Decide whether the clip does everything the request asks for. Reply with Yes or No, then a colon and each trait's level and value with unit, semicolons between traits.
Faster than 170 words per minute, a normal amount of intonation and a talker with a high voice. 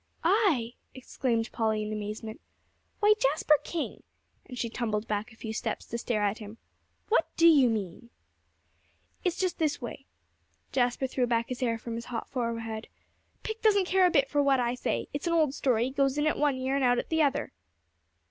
Yes: average, 195 wpm; average, 4.5 semitones; very high, 250 Hz